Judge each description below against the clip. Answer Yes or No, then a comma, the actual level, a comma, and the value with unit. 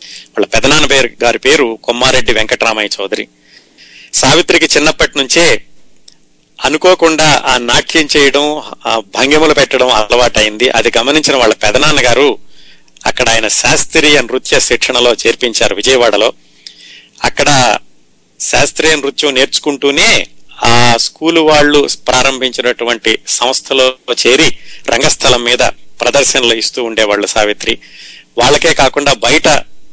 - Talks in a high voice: No, low, 130 Hz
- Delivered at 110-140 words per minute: No, average, 100 wpm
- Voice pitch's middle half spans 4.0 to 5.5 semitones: Yes, average, 4.3 semitones